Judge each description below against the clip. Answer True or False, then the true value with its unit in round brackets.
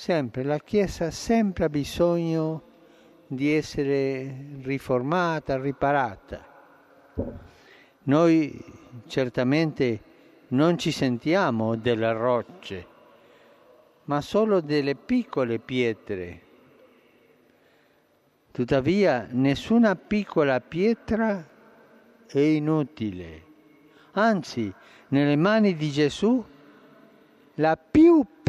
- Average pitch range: True (4.7 semitones)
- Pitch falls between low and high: True (150 Hz)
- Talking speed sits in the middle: False (75 wpm)